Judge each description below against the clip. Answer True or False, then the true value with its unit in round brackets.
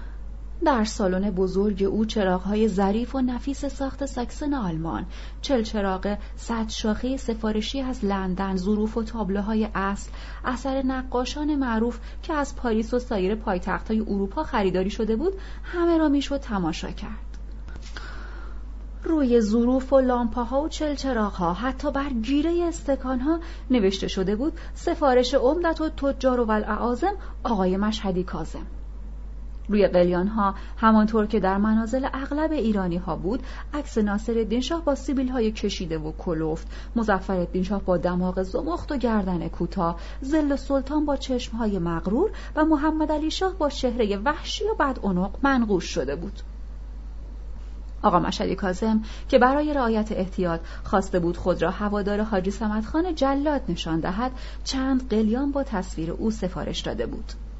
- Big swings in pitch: True (6.1 semitones)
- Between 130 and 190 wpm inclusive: True (140 wpm)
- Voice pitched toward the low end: False (220 Hz)